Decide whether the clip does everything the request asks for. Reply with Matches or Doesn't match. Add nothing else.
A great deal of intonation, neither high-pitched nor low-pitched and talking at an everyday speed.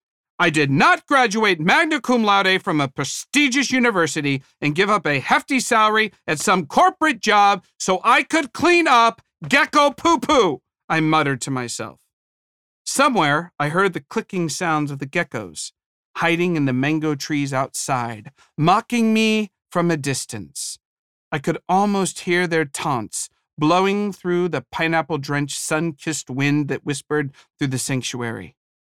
Matches